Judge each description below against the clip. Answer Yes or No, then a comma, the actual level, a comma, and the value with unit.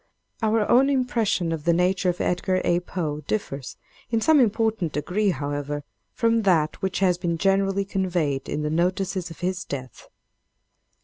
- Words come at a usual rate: Yes, average, 160 wpm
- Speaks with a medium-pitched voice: Yes, medium, 180 Hz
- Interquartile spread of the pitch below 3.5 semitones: No, average, 3.8 semitones